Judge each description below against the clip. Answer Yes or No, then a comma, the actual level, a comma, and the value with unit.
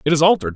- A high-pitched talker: No, medium, 155 Hz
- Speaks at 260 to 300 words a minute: No, fast, 325 wpm